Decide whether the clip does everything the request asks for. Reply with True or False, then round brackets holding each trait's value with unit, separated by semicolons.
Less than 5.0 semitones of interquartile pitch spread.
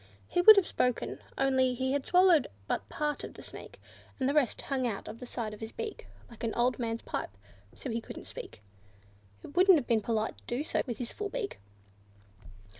True (4.6 semitones)